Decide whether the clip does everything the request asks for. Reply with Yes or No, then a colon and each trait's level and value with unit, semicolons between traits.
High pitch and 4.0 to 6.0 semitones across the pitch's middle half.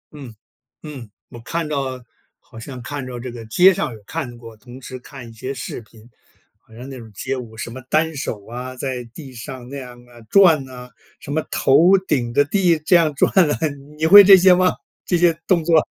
No: low, 130 Hz; average, 4.7 semitones